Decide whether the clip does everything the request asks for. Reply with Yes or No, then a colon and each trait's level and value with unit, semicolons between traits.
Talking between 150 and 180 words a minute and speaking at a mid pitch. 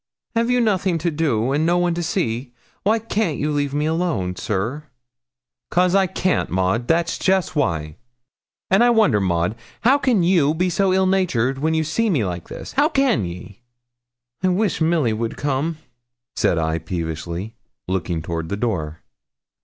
Yes: average, 170 wpm; medium, 150 Hz